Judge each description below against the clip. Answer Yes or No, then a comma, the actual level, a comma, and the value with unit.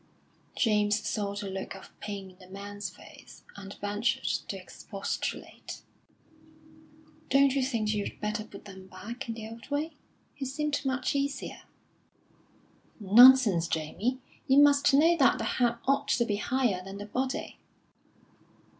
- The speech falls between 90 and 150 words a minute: Yes, average, 145 wpm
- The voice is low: No, high, 220 Hz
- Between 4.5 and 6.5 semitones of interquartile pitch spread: Yes, average, 4.9 semitones